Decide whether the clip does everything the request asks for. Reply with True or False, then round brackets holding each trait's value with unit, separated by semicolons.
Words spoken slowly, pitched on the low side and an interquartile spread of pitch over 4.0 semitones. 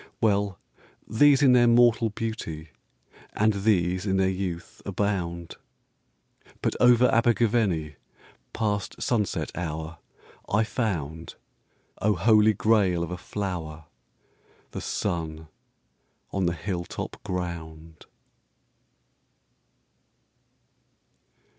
True (90 wpm; 95 Hz; 4.5 semitones)